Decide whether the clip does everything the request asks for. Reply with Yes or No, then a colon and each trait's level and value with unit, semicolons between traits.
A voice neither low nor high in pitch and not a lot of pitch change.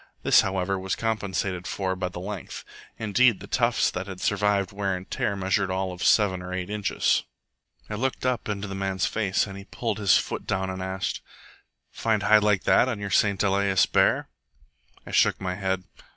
No: low, 100 Hz; narrow, 1.8 semitones